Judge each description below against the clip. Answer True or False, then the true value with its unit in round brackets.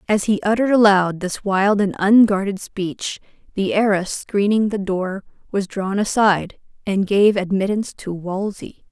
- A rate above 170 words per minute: False (150 wpm)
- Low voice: False (200 Hz)